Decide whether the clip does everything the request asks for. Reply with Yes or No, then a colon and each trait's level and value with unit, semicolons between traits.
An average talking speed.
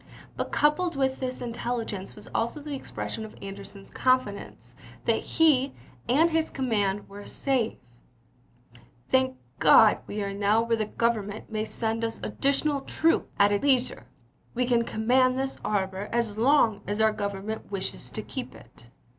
Yes: average, 160 wpm